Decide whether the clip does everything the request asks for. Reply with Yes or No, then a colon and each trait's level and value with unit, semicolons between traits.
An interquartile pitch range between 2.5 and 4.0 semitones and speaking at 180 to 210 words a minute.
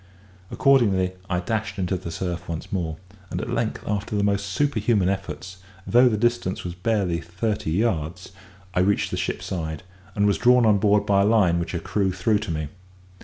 Yes: average, 3.5 semitones; average, 190 wpm